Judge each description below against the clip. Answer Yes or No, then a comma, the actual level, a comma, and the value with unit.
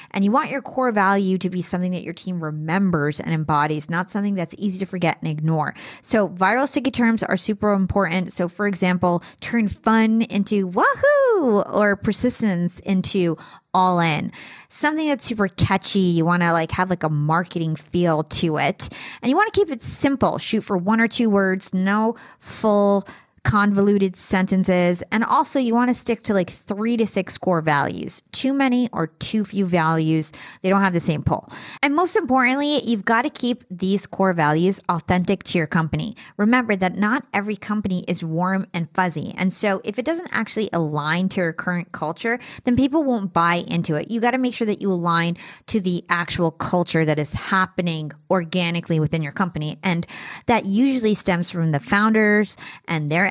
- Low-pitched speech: No, high, 190 Hz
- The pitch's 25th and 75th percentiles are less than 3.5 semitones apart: No, average, 4.4 semitones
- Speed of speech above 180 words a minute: Yes, average, 190 wpm